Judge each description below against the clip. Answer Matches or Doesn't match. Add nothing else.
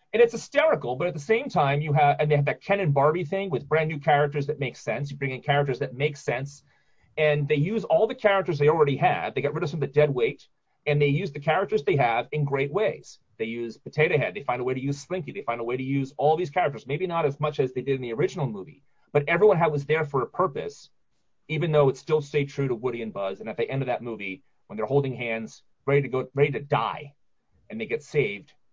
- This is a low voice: Doesn't match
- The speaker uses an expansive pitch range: Doesn't match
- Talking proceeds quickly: Matches